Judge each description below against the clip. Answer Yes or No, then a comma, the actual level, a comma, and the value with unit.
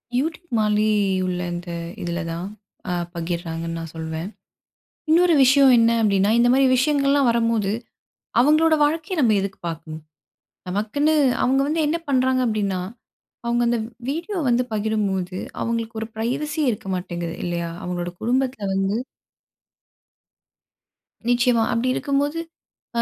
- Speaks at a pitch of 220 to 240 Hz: Yes, high, 230 Hz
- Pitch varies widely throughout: Yes, wide, 6.9 semitones